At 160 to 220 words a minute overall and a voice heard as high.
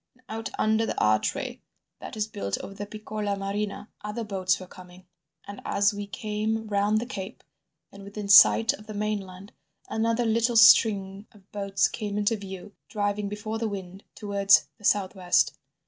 Yes: average, 170 wpm; high, 205 Hz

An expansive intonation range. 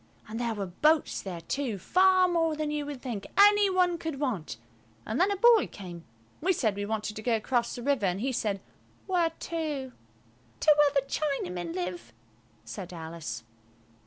Yes: wide, 8.7 semitones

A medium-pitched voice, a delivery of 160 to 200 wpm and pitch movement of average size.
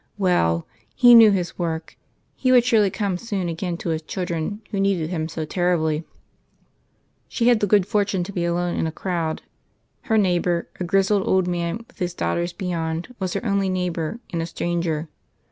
Yes: medium, 180 Hz; average, 180 wpm; average, 3.0 semitones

